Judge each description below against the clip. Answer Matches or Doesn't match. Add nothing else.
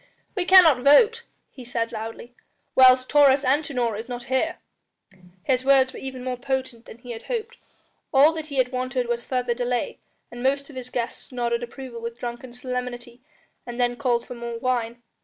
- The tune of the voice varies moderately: Doesn't match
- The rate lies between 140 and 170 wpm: Doesn't match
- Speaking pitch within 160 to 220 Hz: Doesn't match